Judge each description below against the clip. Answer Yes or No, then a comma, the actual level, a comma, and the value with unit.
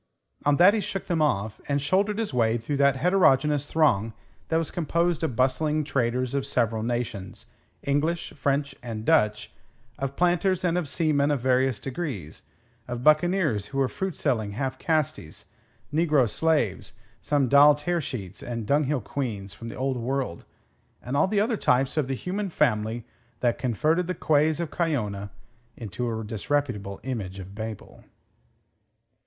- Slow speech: No, average, 155 wpm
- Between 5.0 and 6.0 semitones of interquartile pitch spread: Yes, wide, 5.5 semitones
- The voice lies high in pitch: No, low, 135 Hz